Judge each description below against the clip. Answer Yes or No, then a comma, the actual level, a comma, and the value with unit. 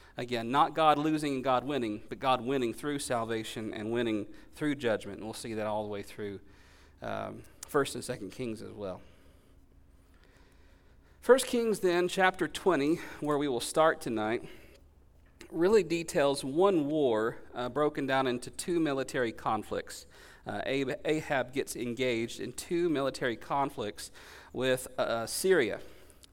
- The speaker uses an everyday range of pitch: No, wide, 6.5 semitones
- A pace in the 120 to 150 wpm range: Yes, average, 145 wpm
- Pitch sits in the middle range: No, low, 125 Hz